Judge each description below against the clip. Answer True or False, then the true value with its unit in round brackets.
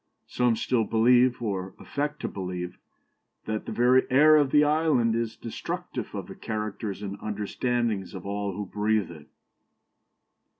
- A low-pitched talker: True (110 Hz)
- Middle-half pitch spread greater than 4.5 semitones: False (3.6 semitones)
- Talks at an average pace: True (145 wpm)